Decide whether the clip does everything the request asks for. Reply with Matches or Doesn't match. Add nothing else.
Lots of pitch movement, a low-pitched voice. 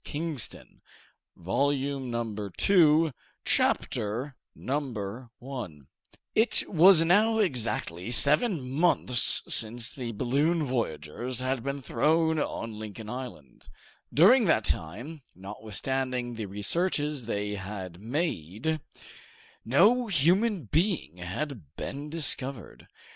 Matches